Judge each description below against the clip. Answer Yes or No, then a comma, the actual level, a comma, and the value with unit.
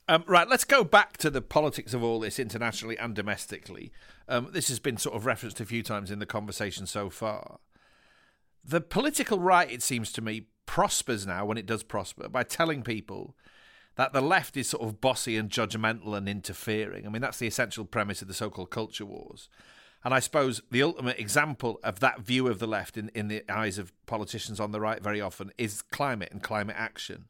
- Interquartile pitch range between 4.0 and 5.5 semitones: No, average, 3.6 semitones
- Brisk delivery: Yes, fast, 210 wpm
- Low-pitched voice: Yes, low, 115 Hz